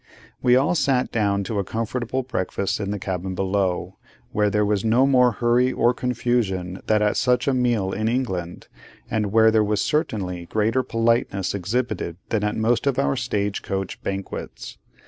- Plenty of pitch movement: No, average, 4.0 semitones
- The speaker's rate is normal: Yes, average, 170 wpm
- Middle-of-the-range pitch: No, low, 110 Hz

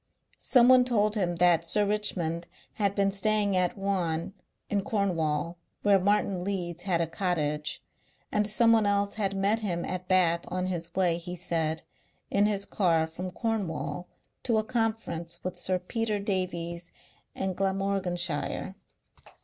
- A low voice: No, medium, 185 Hz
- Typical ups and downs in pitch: Yes, average, 3.1 semitones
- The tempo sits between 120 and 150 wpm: Yes, average, 140 wpm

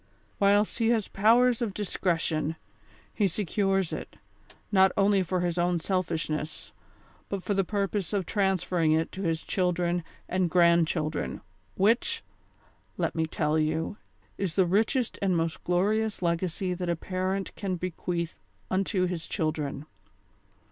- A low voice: No, medium, 185 Hz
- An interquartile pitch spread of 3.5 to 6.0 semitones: No, average, 3.1 semitones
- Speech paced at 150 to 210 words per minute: No, average, 140 wpm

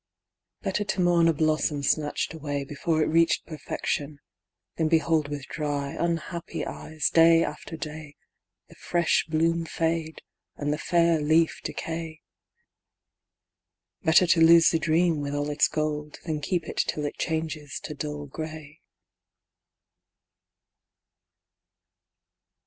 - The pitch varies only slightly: Yes, narrow, 1.9 semitones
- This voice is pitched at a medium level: Yes, medium, 155 Hz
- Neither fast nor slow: No, slow, 125 wpm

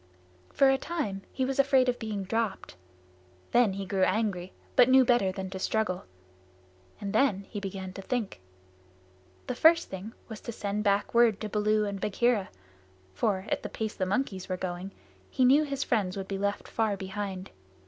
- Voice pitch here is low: No, high, 205 Hz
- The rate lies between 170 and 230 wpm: Yes, average, 180 wpm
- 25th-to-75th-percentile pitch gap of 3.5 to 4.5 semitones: Yes, average, 4.0 semitones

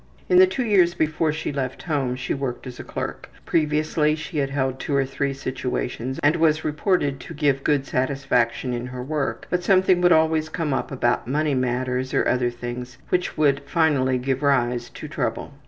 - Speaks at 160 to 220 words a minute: Yes, average, 190 wpm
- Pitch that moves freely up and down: No, average, 3.4 semitones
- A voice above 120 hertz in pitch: Yes, medium, 140 Hz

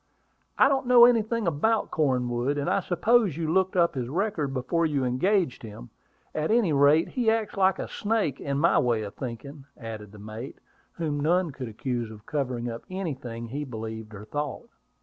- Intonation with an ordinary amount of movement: No, wide, 7.5 semitones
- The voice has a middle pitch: Yes, medium, 145 Hz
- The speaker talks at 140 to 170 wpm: No, average, 185 wpm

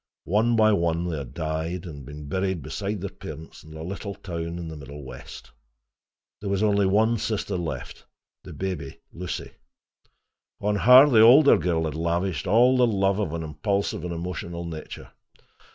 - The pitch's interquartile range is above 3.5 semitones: Yes, average, 4.2 semitones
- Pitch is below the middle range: Yes, very low, 90 Hz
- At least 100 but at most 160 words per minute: No, average, 170 wpm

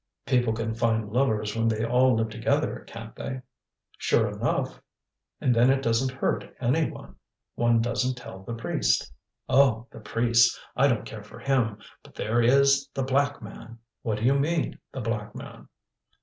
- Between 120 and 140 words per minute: No, average, 170 wpm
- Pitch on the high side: No, low, 120 Hz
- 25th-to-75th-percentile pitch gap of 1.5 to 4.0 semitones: Yes, average, 2.8 semitones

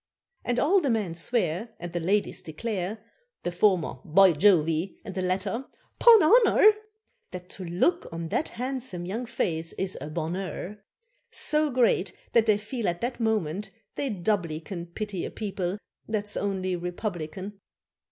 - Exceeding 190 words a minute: No, average, 150 wpm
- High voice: Yes, high, 195 Hz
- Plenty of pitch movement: No, average, 4.6 semitones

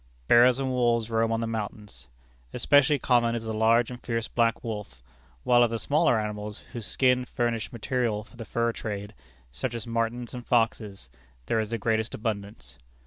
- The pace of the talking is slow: No, average, 180 wpm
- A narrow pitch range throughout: Yes, narrow, 1.9 semitones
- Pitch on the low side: Yes, low, 115 Hz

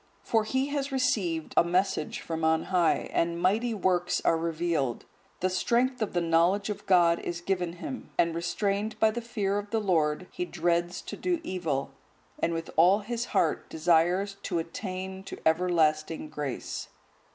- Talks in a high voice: No, medium, 180 Hz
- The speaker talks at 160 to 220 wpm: Yes, average, 165 wpm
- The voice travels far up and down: No, average, 3.8 semitones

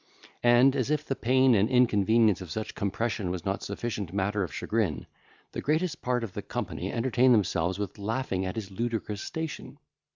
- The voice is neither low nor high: No, low, 110 Hz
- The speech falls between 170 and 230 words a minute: Yes, average, 175 wpm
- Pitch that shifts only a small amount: No, average, 4.3 semitones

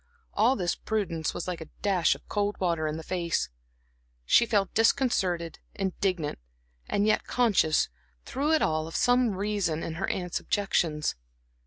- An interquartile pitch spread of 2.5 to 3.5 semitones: No, average, 4.3 semitones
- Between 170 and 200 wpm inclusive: No, average, 155 wpm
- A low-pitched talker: No, medium, 185 Hz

